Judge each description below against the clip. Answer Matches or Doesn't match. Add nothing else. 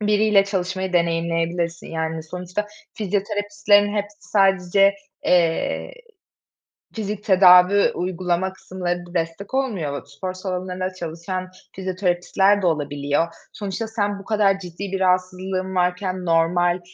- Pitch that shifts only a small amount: Matches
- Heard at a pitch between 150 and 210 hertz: Matches